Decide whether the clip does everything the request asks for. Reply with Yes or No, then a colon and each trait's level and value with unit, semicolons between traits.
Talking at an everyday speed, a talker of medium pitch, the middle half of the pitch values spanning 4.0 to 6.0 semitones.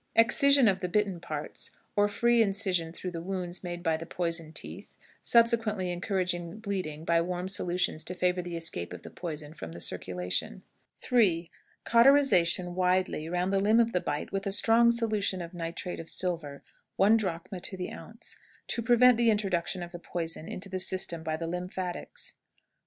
No: average, 180 wpm; medium, 180 Hz; average, 3.5 semitones